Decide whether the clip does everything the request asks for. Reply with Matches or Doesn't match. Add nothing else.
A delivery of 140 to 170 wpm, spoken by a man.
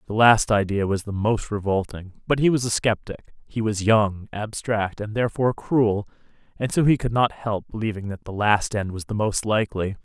Doesn't match